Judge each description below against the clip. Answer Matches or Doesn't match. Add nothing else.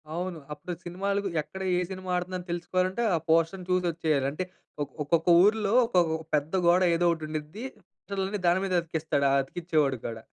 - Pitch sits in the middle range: Matches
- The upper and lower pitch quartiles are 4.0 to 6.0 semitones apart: Doesn't match